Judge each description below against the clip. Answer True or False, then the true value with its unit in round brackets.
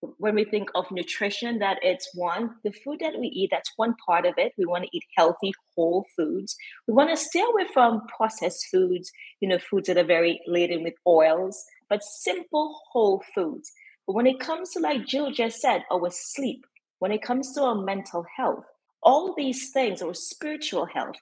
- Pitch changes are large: True (7.5 semitones)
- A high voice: True (215 Hz)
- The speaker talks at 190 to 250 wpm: True (200 wpm)